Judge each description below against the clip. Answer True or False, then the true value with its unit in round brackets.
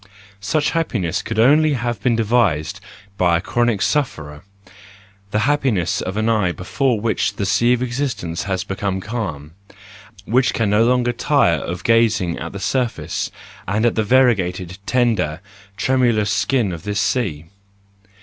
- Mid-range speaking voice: False (110 Hz)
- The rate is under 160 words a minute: True (150 wpm)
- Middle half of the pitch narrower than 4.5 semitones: False (4.9 semitones)